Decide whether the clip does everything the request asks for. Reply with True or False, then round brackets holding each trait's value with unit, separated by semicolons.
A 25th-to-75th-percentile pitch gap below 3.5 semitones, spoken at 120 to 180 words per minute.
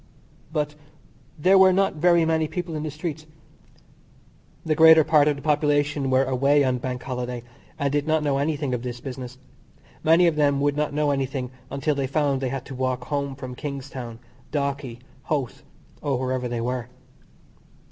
True (2.8 semitones; 175 wpm)